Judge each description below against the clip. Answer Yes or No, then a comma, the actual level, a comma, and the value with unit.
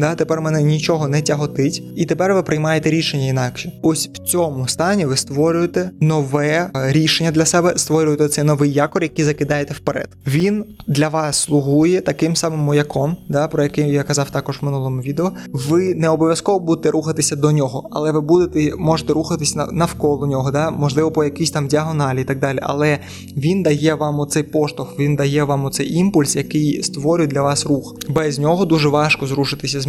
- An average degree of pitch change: No, narrow, 2.1 semitones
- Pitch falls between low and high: Yes, medium, 150 Hz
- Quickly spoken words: Yes, fast, 180 wpm